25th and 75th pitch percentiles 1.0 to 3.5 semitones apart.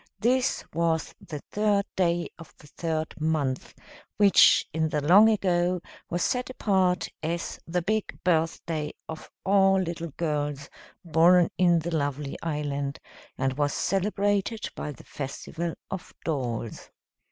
No: average, 4.1 semitones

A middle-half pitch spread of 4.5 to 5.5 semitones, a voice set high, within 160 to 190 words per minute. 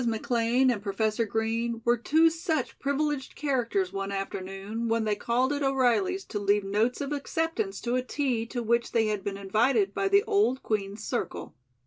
Yes: average, 4.8 semitones; high, 235 Hz; average, 175 wpm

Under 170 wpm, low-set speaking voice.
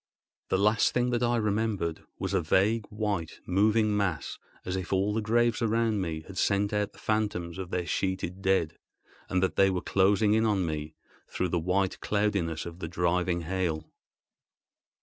No: average, 175 wpm; very low, 95 Hz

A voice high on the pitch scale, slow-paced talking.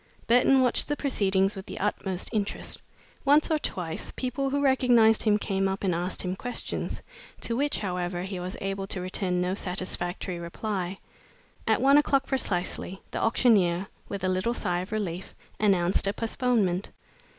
No: high, 195 Hz; average, 160 wpm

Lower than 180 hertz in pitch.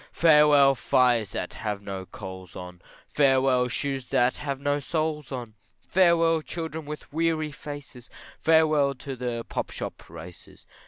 Yes: medium, 140 Hz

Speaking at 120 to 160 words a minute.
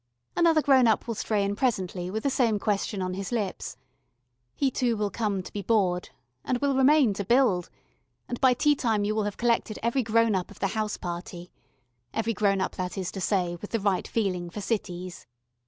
No: fast, 205 wpm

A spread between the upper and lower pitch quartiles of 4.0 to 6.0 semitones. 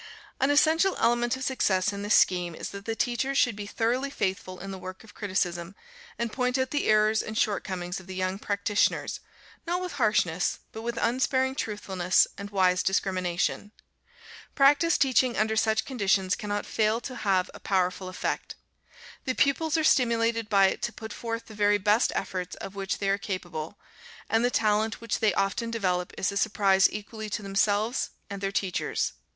No: average, 3.5 semitones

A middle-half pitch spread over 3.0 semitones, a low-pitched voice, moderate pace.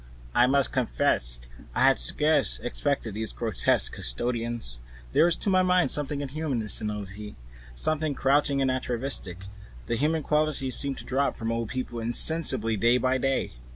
Yes: average, 4.2 semitones; low, 130 Hz; average, 155 wpm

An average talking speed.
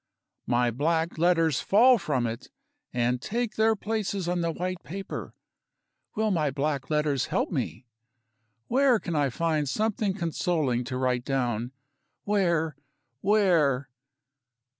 No: slow, 125 wpm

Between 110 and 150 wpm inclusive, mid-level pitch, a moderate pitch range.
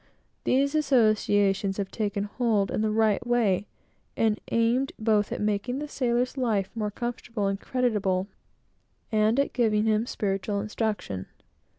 No: slow, 135 wpm; high, 215 Hz; average, 3.0 semitones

